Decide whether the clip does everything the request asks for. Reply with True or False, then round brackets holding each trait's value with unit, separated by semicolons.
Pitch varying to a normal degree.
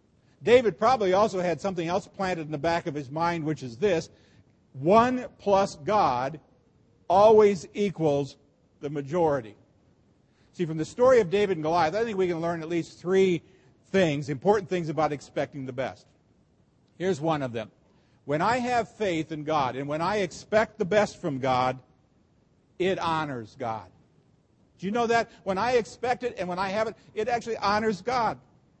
False (5.8 semitones)